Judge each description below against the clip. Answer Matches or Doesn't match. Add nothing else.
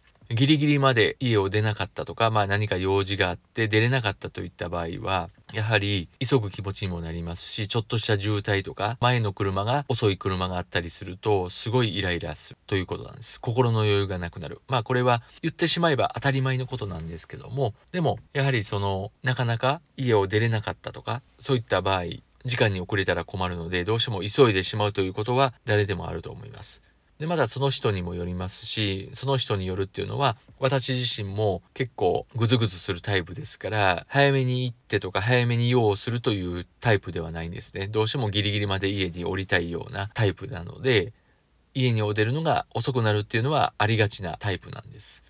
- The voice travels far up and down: Doesn't match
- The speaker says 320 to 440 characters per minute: Matches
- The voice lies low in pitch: Matches